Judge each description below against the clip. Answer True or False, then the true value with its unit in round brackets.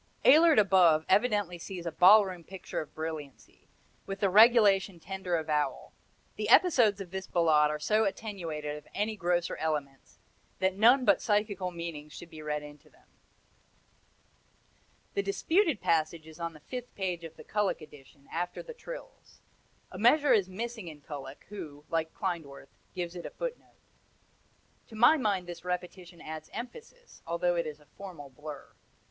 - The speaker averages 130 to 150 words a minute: False (160 wpm)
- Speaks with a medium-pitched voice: True (180 Hz)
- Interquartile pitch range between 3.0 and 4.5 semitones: False (4.9 semitones)